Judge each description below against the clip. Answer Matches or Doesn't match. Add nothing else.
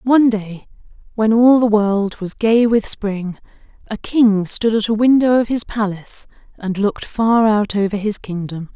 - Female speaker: Matches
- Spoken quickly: Doesn't match